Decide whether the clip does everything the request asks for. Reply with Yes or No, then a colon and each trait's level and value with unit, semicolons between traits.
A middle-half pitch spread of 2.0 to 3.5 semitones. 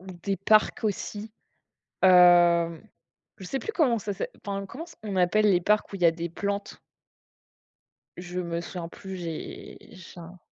Yes: average, 3.0 semitones